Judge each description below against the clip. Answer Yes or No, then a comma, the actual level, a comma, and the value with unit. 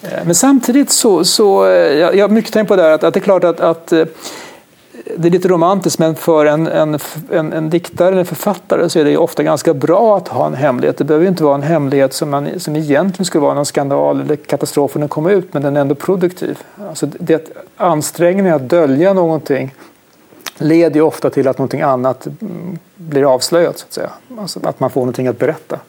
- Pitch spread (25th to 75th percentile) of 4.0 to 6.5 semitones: No, average, 3.3 semitones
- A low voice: No, medium, 160 Hz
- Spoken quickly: Yes, fast, 210 wpm